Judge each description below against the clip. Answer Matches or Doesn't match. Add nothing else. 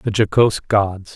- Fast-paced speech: Doesn't match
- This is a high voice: Doesn't match